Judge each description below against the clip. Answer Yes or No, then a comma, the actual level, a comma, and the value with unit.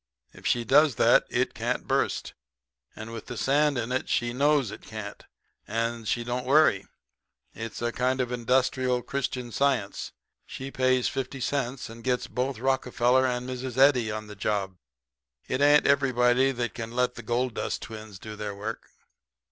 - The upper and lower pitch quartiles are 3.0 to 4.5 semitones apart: No, narrow, 2.4 semitones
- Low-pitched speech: Yes, low, 125 Hz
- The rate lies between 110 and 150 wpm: No, average, 170 wpm